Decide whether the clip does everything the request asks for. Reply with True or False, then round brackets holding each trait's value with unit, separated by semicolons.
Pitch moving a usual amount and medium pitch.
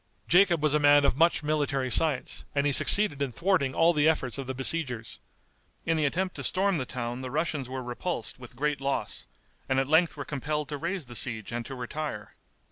True (3.7 semitones; 145 Hz)